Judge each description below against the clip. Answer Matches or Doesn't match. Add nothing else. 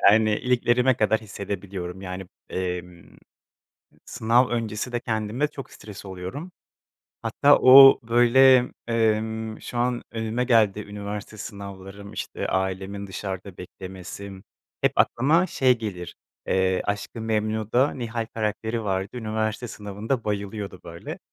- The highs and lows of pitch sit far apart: Doesn't match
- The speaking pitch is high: Doesn't match